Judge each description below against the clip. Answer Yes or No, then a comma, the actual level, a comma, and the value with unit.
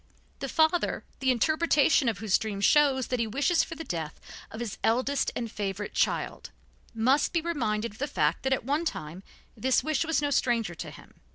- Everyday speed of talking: Yes, average, 195 wpm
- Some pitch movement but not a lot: No, wide, 5.7 semitones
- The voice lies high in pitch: Yes, very high, 255 Hz